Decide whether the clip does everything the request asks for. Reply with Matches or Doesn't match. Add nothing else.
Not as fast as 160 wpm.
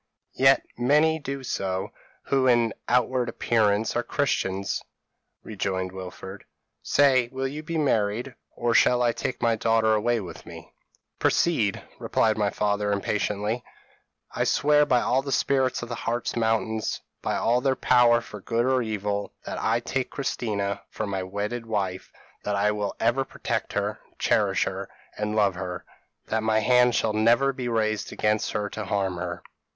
Doesn't match